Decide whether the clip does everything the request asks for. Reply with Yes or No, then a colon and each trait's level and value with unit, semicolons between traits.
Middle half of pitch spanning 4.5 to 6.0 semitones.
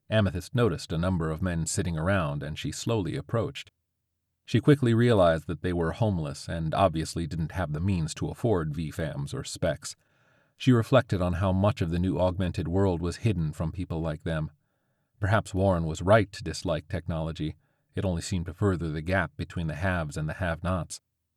Yes: average, 4.8 semitones